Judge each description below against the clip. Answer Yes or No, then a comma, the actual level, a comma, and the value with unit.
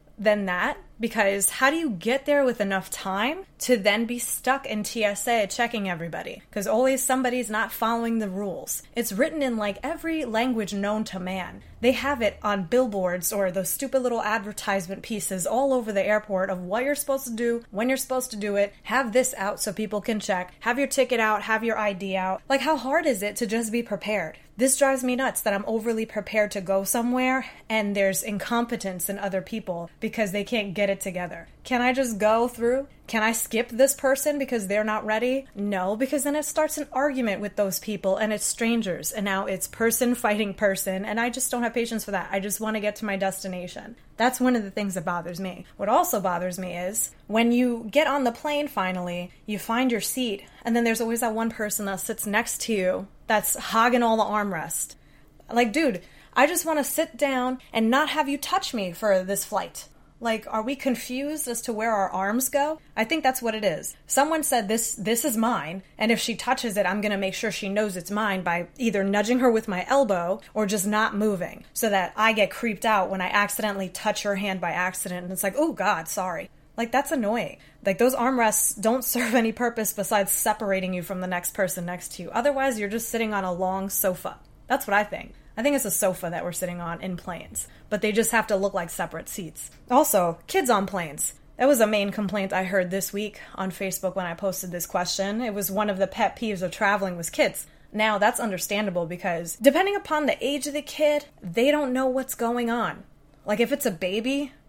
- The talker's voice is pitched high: Yes, high, 215 Hz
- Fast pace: Yes, fast, 220 wpm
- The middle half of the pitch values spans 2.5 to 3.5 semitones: No, average, 4.1 semitones